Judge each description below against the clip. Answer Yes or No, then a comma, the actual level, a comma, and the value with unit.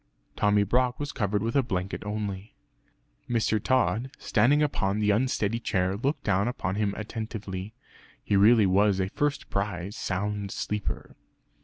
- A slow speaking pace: No, average, 145 wpm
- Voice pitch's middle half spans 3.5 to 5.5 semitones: No, average, 3.0 semitones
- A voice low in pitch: Yes, low, 105 Hz